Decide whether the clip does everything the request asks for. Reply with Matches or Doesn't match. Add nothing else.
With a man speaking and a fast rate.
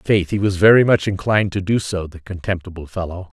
Matches